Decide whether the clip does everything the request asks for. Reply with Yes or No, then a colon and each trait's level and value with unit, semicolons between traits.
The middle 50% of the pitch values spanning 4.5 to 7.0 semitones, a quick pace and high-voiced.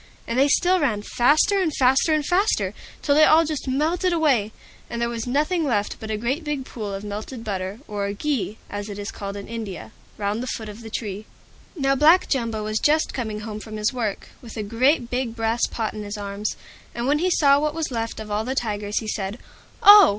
Yes: wide, 5.6 semitones; fast, 225 wpm; high, 235 Hz